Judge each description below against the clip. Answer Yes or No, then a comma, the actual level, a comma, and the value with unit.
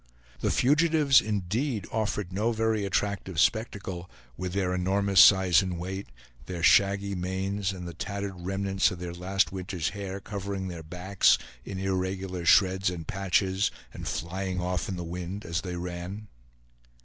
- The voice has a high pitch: No, very low, 95 Hz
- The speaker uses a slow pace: No, average, 150 wpm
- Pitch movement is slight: Yes, narrow, 1.9 semitones